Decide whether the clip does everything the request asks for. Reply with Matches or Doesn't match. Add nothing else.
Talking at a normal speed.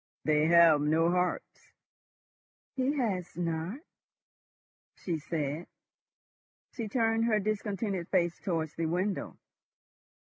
Doesn't match